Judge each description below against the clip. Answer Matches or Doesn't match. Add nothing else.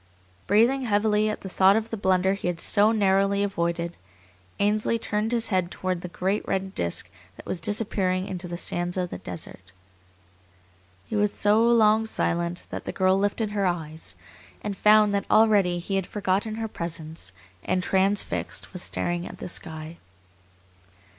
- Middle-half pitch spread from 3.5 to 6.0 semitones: Doesn't match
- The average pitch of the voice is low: Doesn't match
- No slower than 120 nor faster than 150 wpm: Doesn't match